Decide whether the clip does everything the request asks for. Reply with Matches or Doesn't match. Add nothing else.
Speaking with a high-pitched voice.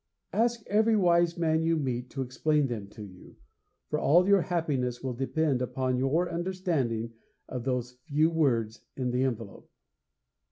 Doesn't match